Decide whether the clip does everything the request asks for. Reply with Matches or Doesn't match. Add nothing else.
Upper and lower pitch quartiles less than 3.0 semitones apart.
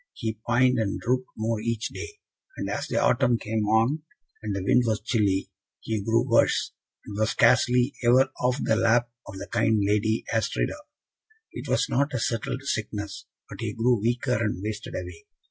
Matches